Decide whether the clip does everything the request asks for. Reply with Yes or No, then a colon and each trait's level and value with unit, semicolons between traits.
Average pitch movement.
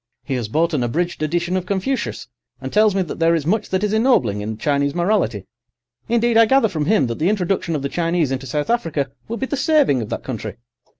No: wide, 7.4 semitones